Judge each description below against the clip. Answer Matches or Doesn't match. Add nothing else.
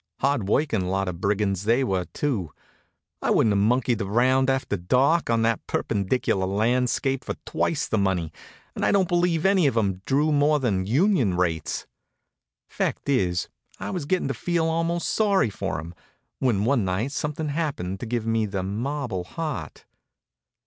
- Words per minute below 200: Matches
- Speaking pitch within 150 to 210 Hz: Doesn't match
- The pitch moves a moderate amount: Doesn't match